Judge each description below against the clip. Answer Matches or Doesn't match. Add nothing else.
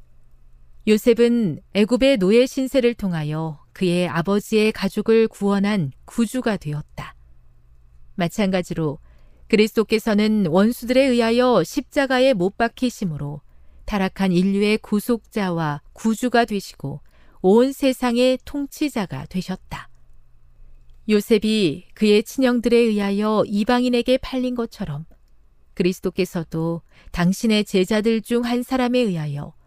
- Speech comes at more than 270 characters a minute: Doesn't match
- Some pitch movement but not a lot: Doesn't match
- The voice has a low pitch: Doesn't match